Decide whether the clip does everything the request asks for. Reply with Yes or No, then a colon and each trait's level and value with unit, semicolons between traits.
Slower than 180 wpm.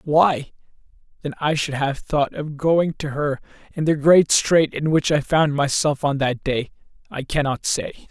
No: average, 185 wpm